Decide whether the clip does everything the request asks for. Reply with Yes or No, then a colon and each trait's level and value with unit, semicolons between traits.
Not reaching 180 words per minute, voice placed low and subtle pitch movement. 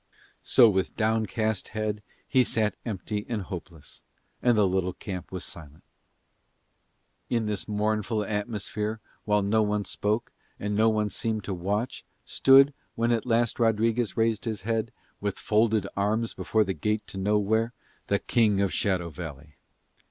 Yes: average, 150 wpm; low, 105 Hz; narrow, 2.2 semitones